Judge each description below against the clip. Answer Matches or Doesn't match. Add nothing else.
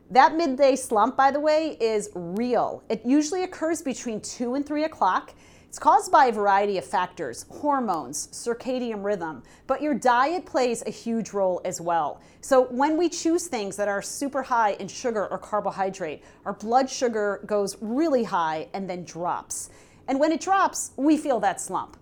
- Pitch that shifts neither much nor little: Doesn't match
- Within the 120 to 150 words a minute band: Doesn't match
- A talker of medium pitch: Doesn't match